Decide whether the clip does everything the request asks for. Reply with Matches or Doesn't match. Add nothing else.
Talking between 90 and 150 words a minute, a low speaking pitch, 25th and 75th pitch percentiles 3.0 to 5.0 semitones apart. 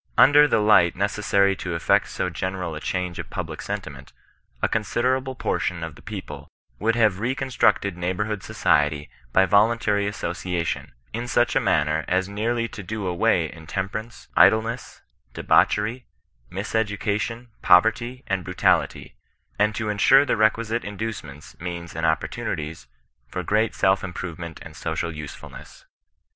Matches